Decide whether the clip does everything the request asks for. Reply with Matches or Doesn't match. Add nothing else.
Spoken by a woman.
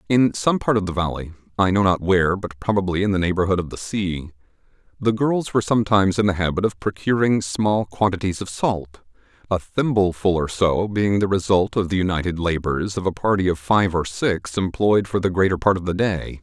Doesn't match